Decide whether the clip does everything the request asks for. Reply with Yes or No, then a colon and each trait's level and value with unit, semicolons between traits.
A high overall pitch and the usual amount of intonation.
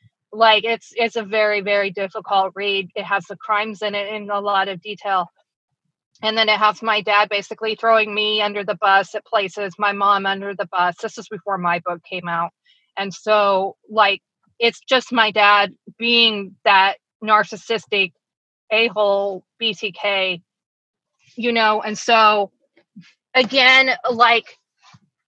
No: high, 210 Hz; narrow, 2.0 semitones